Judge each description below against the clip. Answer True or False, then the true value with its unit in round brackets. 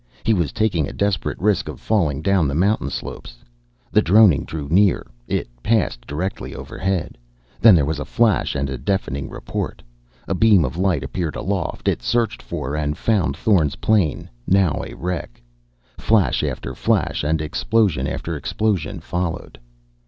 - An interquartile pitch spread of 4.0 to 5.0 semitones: False (5.4 semitones)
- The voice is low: True (90 Hz)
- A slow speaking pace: False (160 wpm)